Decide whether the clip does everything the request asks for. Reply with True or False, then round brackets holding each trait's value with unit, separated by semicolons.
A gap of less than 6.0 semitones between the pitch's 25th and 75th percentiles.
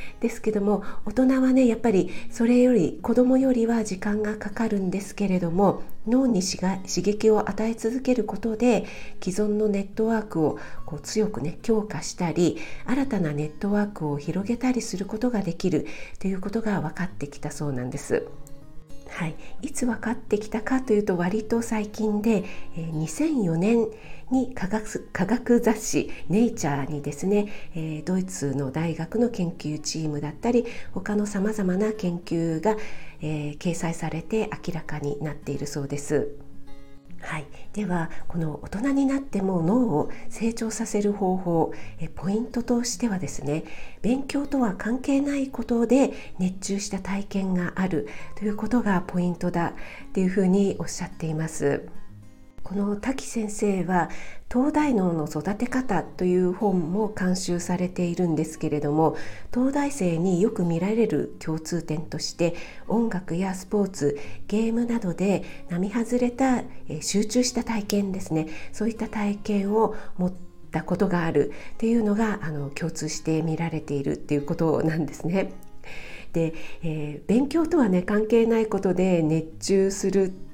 True (5.6 semitones)